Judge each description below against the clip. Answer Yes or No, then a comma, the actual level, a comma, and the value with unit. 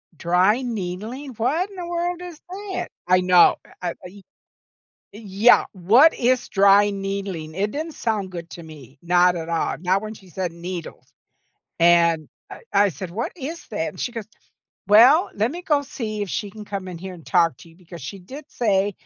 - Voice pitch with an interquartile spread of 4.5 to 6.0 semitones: Yes, wide, 5.6 semitones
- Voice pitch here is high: Yes, high, 200 Hz